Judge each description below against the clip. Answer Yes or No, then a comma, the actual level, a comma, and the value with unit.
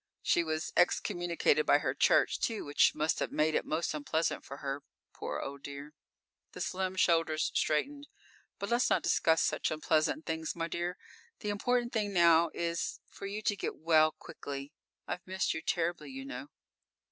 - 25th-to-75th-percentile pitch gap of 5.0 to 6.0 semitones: No, average, 4.1 semitones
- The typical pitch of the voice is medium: Yes, medium, 170 Hz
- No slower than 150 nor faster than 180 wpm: Yes, average, 170 wpm